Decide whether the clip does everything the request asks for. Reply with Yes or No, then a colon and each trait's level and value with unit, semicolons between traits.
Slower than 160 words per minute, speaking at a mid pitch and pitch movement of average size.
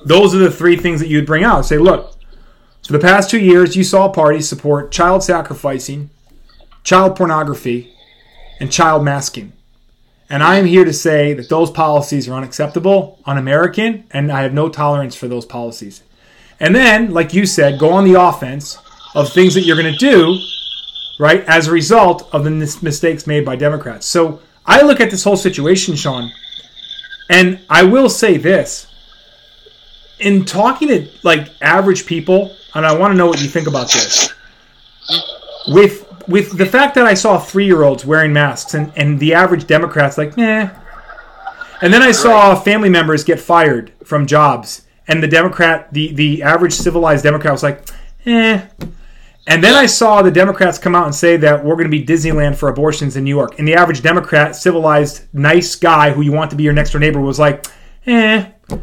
No: average, 185 wpm; medium, 165 Hz; average, 4.2 semitones